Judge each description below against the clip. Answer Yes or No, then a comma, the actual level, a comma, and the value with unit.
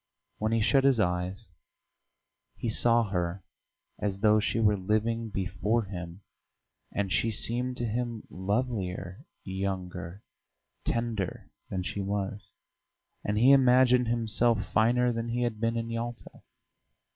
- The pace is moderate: No, slow, 130 wpm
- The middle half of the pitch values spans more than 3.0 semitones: Yes, average, 3.4 semitones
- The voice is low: Yes, low, 110 Hz